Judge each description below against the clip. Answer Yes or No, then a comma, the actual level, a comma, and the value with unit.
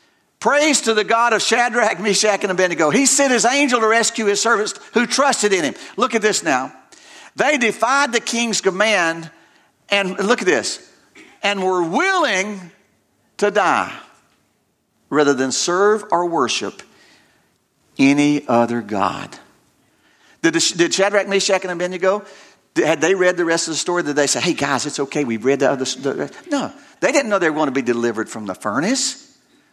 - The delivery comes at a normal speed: Yes, average, 170 wpm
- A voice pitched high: Yes, high, 200 Hz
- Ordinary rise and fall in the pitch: No, wide, 6.4 semitones